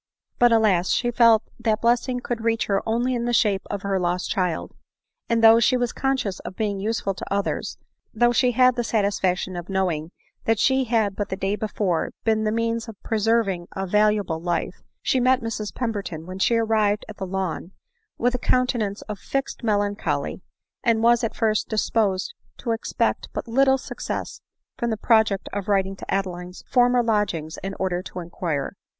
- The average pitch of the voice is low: No, high, 215 Hz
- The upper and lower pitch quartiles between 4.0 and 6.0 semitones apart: No, average, 3.4 semitones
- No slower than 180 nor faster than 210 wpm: Yes, average, 190 wpm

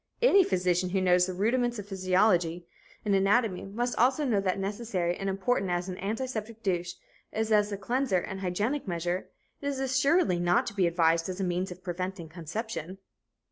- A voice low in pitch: No, high, 195 Hz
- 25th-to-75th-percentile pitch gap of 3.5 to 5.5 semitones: Yes, average, 3.9 semitones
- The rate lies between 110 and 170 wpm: No, average, 185 wpm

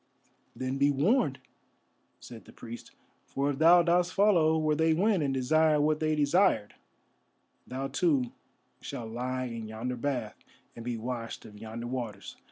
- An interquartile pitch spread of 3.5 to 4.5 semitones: No, average, 4.9 semitones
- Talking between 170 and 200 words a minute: No, average, 155 wpm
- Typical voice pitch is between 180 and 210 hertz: No, low, 135 Hz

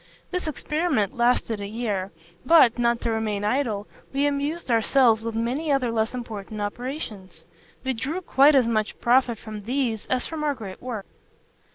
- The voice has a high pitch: Yes, high, 235 Hz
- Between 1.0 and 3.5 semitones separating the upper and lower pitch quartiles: No, average, 4.1 semitones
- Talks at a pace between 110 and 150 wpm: No, average, 165 wpm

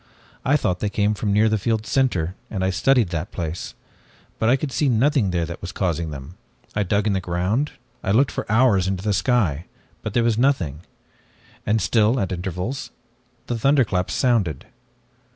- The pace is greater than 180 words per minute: Yes, average, 190 wpm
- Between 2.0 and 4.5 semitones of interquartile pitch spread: No, average, 4.9 semitones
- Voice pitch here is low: Yes, low, 105 Hz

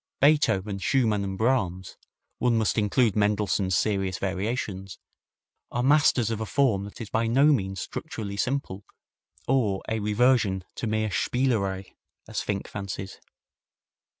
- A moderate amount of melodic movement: Yes, average, 3.9 semitones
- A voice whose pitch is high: No, low, 105 Hz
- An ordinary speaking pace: No, slow, 130 wpm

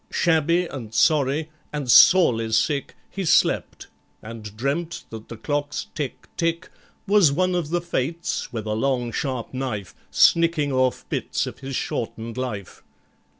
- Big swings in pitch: Yes, wide, 6.2 semitones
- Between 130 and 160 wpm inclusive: Yes, average, 145 wpm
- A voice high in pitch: No, medium, 140 Hz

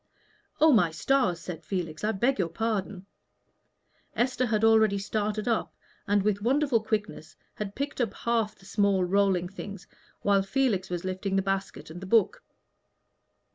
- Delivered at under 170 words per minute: Yes, average, 155 wpm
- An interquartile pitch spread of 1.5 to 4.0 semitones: Yes, average, 2.9 semitones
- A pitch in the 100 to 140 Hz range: No, high, 205 Hz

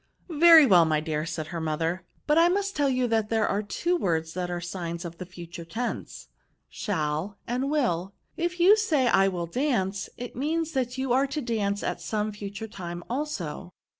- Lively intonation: Yes, wide, 8.1 semitones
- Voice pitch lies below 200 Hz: No, high, 210 Hz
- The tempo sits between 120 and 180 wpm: No, fast, 205 wpm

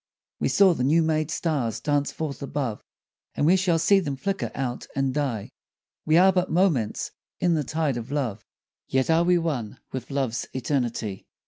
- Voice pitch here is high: No, medium, 145 Hz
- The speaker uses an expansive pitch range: No, average, 4.7 semitones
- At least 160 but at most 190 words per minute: Yes, average, 180 wpm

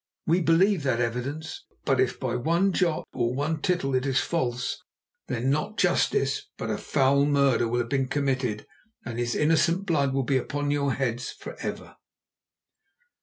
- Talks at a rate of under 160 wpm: No, average, 170 wpm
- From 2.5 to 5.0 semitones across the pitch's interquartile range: Yes, average, 4.0 semitones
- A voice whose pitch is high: No, medium, 140 Hz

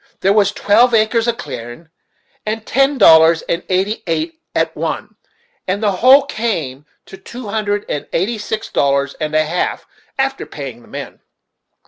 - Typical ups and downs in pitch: No, wide, 6.3 semitones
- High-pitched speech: Yes, high, 205 Hz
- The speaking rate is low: No, average, 160 wpm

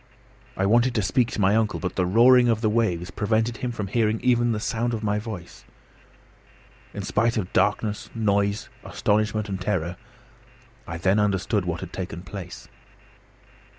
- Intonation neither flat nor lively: Yes, average, 3.0 semitones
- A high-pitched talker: No, low, 105 Hz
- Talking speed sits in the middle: Yes, average, 165 wpm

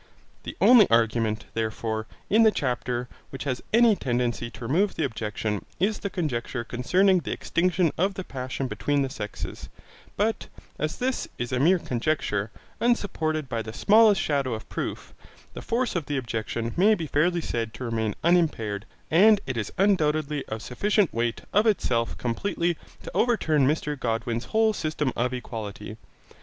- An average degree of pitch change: No, wide, 7.9 semitones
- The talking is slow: No, average, 160 wpm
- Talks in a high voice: No, medium, 140 Hz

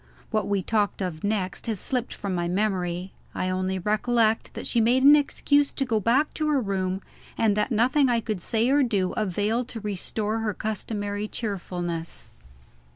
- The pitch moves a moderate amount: Yes, average, 3.9 semitones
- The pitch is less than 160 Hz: No, high, 215 Hz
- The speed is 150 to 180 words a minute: Yes, average, 175 wpm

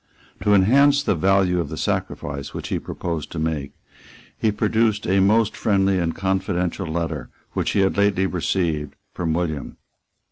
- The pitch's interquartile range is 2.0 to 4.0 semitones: Yes, average, 3.7 semitones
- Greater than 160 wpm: No, average, 155 wpm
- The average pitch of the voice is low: Yes, very low, 95 Hz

